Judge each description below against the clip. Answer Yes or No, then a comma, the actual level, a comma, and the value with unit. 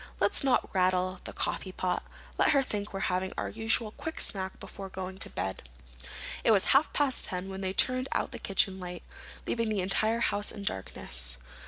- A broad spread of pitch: No, average, 3.2 semitones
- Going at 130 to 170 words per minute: No, average, 185 wpm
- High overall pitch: Yes, high, 195 Hz